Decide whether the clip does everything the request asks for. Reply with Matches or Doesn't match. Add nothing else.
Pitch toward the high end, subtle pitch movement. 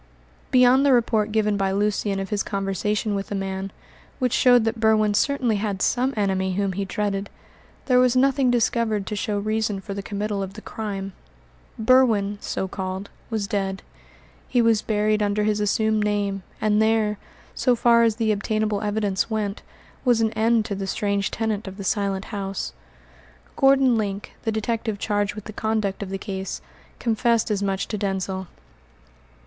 Matches